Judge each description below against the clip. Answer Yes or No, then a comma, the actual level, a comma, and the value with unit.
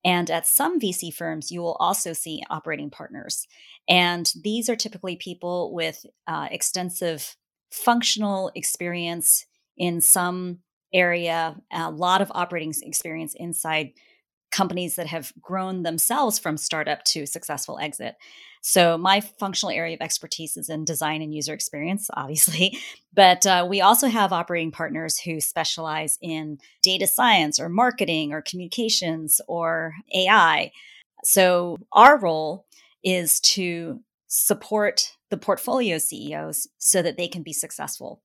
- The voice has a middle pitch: Yes, medium, 175 Hz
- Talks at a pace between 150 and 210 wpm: No, slow, 135 wpm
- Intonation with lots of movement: No, average, 3.0 semitones